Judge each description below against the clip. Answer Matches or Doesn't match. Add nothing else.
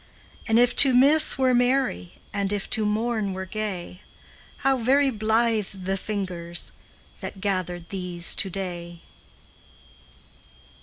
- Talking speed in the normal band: Doesn't match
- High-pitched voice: Matches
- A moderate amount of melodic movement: Matches